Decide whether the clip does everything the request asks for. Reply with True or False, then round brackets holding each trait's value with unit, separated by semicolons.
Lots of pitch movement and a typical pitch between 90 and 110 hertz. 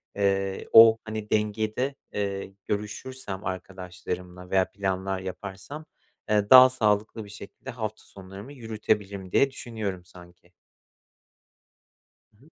False (2.5 semitones; 100 Hz)